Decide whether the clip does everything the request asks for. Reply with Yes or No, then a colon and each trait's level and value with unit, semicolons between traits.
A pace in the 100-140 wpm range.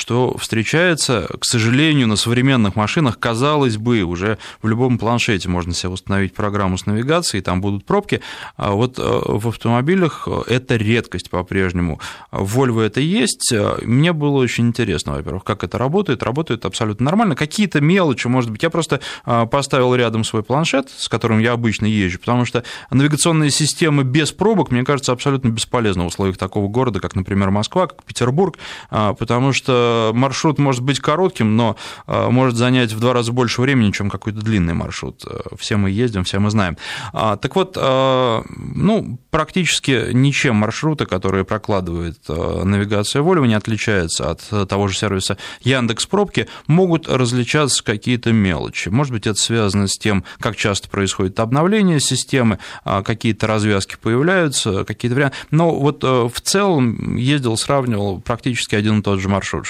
No: average, 155 wpm